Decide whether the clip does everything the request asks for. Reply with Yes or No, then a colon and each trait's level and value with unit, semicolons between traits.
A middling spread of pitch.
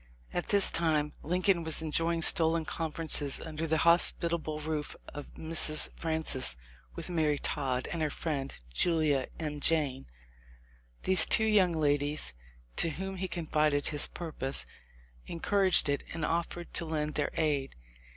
No: narrow, 2.3 semitones